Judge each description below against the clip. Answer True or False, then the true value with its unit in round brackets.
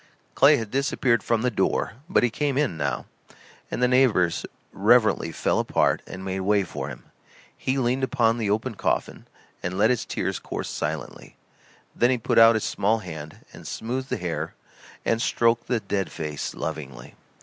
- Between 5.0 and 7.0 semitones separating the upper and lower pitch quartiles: True (5.4 semitones)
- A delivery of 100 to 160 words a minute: False (175 wpm)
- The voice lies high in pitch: False (115 Hz)